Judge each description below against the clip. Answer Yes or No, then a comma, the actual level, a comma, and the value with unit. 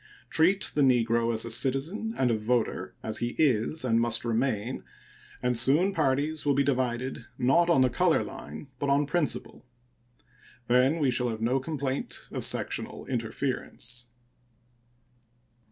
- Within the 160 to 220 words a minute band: No, average, 145 wpm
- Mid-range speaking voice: No, low, 130 Hz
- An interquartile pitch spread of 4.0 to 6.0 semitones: No, average, 3.3 semitones